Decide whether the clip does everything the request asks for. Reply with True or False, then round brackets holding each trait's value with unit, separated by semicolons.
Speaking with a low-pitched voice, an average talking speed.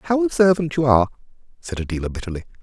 True (120 Hz; 160 wpm)